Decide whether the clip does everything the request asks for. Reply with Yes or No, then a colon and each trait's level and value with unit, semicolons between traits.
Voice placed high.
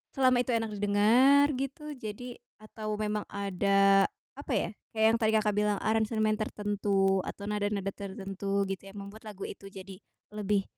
Yes: high, 210 Hz